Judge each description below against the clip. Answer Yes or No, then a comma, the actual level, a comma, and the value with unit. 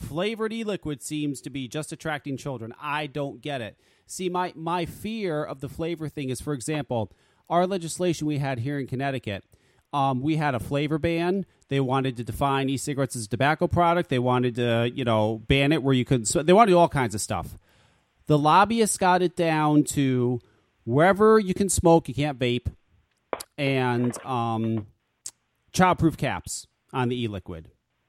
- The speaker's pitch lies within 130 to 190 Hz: Yes, medium, 140 Hz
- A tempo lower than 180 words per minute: No, average, 185 wpm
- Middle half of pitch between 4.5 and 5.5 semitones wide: Yes, average, 4.8 semitones